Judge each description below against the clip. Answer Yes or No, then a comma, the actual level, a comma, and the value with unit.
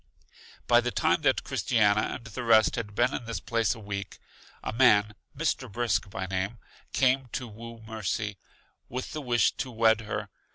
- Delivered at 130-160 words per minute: No, average, 175 wpm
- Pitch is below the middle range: Yes, low, 115 Hz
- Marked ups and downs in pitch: No, narrow, 2.5 semitones